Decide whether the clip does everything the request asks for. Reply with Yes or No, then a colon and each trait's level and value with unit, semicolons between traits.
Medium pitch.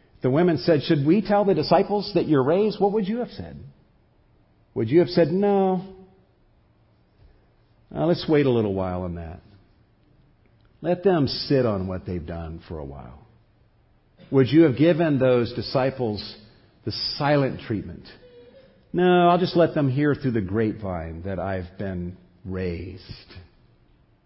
No: low, 120 Hz